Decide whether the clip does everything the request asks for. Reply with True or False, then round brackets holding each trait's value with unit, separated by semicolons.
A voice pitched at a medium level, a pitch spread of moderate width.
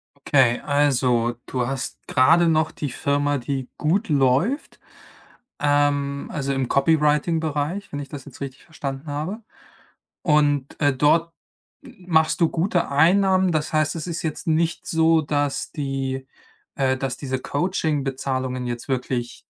True (145 Hz; 3.1 semitones)